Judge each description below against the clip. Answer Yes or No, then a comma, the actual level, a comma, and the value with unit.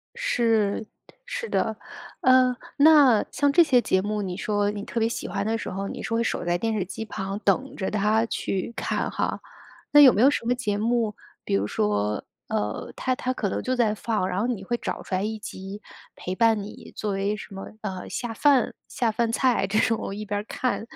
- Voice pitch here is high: Yes, high, 215 Hz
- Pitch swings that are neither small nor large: Yes, average, 3.6 semitones